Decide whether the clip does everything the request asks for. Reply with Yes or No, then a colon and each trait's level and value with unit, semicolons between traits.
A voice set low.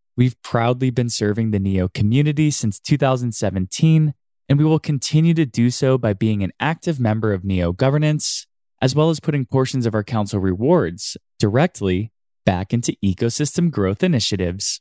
Yes: low, 120 Hz